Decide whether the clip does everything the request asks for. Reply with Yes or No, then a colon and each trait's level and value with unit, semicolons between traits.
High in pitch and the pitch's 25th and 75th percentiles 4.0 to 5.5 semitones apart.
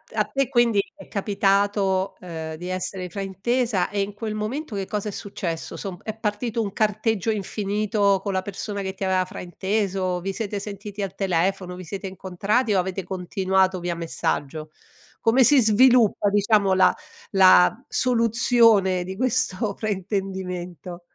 No: high, 195 Hz; narrow, 2.5 semitones